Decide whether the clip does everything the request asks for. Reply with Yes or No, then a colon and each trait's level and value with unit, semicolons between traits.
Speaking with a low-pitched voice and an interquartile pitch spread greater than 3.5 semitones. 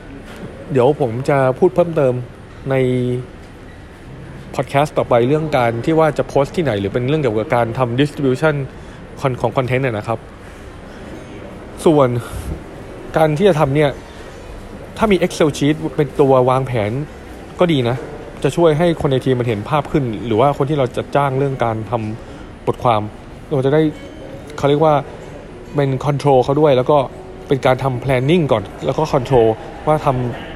Yes: low, 130 Hz; average, 3.9 semitones